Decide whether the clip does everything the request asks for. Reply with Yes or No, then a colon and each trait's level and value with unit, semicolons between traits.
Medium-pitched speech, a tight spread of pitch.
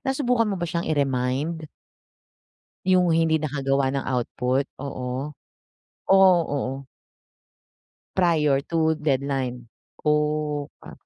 No: medium, 150 Hz; average, 3.5 semitones